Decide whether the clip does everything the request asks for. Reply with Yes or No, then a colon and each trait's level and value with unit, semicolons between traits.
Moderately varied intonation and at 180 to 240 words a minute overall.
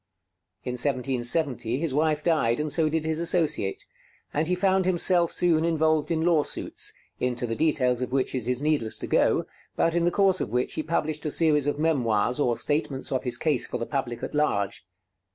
Yes: average, 4.5 semitones; average, 195 wpm